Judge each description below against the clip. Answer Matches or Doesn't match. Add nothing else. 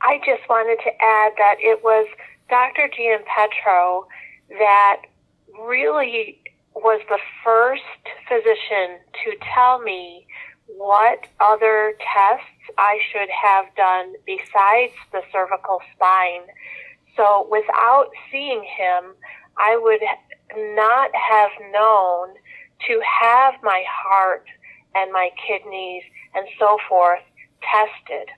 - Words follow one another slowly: Matches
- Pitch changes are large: Doesn't match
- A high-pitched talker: Matches